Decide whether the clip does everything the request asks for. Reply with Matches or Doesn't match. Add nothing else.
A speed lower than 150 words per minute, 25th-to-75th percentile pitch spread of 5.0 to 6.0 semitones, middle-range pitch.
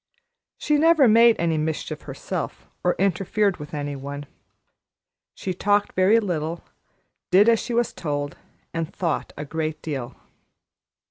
Matches